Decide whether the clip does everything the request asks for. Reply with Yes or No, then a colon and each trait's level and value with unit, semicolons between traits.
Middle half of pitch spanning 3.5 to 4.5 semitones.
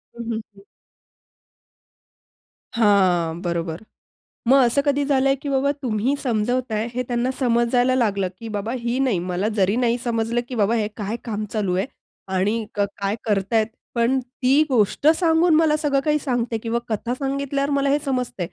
Yes: average, 4.2 semitones